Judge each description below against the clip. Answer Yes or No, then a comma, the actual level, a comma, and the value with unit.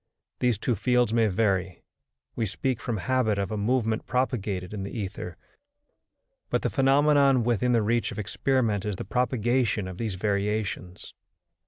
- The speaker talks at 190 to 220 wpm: No, average, 155 wpm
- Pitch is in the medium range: No, low, 110 Hz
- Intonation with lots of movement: No, average, 3.9 semitones